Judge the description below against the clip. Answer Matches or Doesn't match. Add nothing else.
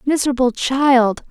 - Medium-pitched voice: Doesn't match